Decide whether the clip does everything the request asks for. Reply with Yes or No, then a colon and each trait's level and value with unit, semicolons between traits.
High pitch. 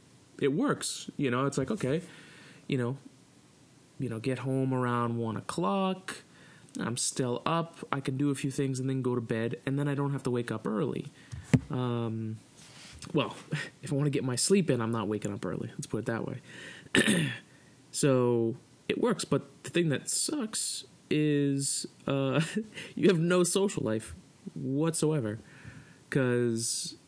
No: medium, 140 Hz